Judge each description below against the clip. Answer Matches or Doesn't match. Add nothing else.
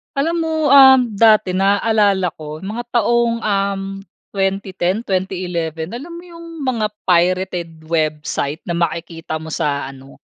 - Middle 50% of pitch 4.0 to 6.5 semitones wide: Matches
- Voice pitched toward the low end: Doesn't match